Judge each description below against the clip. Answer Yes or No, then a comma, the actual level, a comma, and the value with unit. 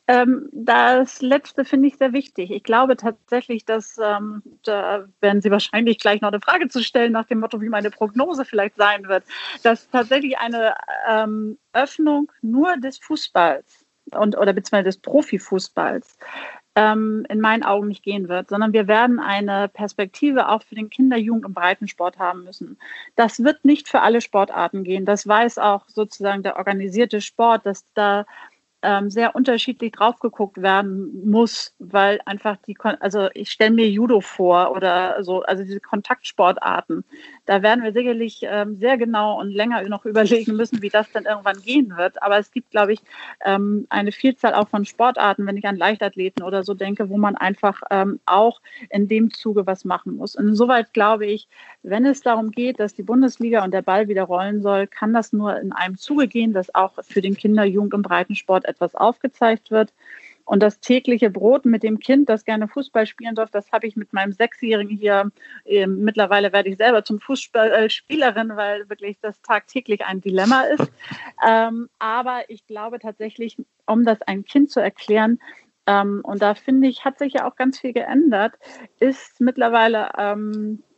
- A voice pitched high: Yes, high, 215 Hz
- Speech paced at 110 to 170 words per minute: No, average, 180 wpm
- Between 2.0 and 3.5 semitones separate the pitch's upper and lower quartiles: Yes, average, 2.9 semitones